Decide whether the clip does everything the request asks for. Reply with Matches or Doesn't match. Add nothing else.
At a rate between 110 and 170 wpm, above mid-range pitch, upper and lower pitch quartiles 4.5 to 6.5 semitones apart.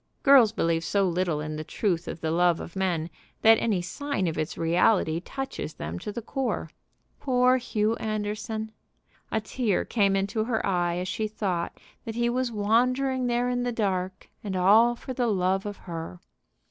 Doesn't match